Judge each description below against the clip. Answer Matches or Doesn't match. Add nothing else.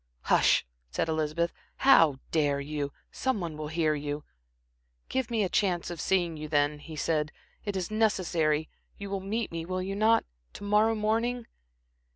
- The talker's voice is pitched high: Doesn't match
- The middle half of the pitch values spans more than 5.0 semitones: Matches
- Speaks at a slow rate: Doesn't match